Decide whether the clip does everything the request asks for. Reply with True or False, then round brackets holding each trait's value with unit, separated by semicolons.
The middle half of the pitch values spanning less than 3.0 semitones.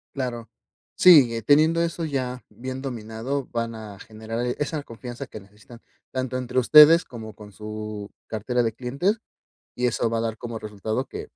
False (3.3 semitones)